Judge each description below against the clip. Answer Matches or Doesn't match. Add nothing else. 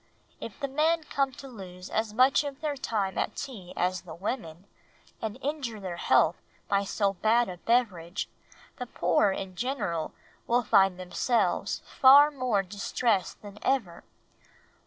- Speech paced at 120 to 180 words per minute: Matches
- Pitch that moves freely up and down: Matches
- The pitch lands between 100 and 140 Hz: Doesn't match